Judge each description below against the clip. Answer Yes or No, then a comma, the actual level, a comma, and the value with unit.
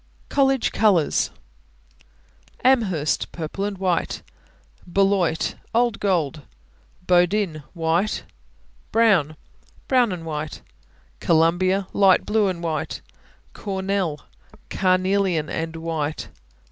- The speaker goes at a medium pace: No, slow, 85 wpm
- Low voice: No, medium, 185 Hz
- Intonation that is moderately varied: Yes, average, 3.6 semitones